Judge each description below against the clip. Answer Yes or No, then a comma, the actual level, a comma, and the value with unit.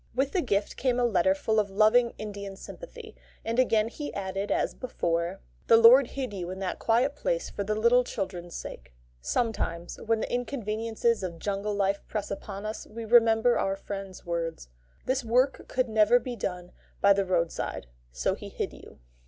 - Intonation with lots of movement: No, average, 3.8 semitones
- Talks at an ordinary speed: Yes, average, 185 wpm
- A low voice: No, high, 215 Hz